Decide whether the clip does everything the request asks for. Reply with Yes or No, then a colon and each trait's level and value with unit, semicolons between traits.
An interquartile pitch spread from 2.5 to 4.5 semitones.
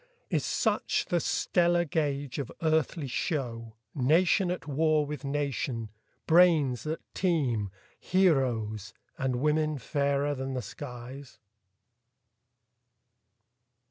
Yes: average, 4.0 semitones